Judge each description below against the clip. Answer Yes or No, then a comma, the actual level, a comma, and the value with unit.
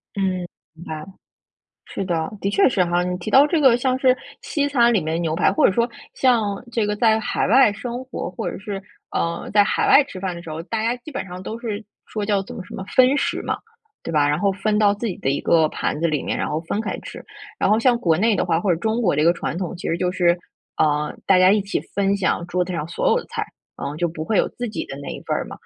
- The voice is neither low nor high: No, high, 195 Hz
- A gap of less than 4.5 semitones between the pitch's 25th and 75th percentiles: No, average, 4.8 semitones